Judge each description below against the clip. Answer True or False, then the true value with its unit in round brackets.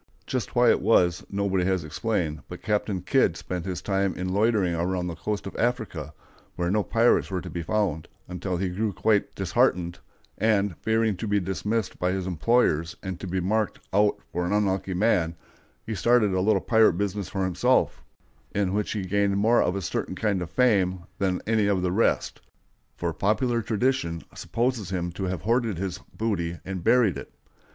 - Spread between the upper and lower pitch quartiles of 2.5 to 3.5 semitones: True (3.2 semitones)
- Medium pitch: False (95 Hz)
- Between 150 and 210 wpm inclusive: True (185 wpm)